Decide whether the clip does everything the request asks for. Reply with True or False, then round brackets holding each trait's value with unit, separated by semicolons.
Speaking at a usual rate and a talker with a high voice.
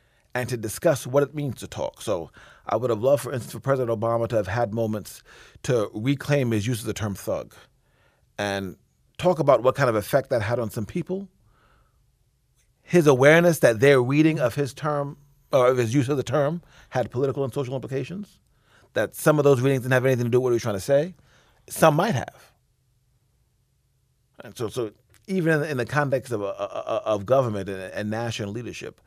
False (195 wpm; 125 Hz)